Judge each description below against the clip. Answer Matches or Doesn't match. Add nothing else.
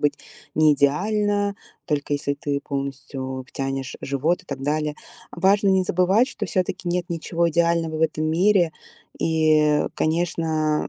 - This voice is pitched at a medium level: Matches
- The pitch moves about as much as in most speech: Matches